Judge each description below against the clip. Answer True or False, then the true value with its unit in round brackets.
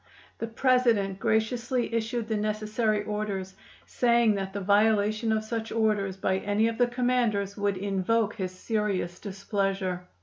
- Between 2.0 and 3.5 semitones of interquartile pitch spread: True (2.6 semitones)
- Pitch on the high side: True (215 Hz)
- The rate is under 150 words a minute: True (140 wpm)